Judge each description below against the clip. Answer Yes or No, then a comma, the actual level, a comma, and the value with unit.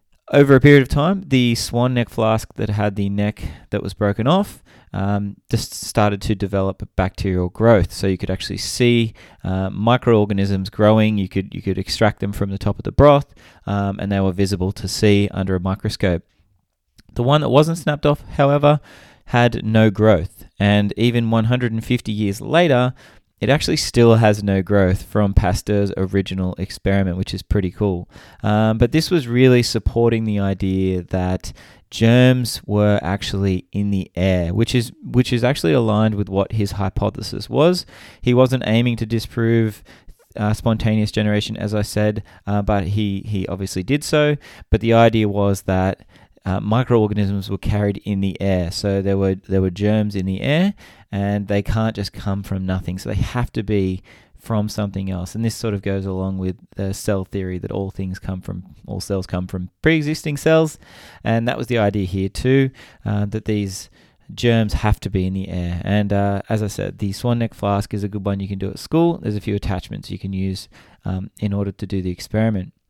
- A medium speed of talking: Yes, average, 190 wpm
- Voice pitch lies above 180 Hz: No, low, 105 Hz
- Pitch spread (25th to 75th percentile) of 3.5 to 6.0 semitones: No, average, 3.1 semitones